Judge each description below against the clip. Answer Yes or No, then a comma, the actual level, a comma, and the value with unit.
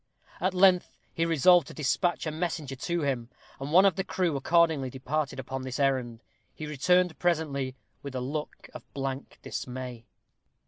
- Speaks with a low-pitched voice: No, medium, 150 Hz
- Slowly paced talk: No, average, 165 wpm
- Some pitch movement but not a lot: Yes, average, 4.6 semitones